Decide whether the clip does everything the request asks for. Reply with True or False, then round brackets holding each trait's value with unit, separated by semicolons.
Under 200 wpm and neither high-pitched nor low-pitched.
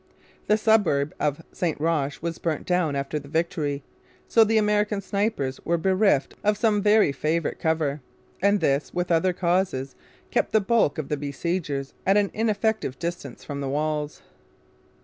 True (160 wpm; 170 Hz)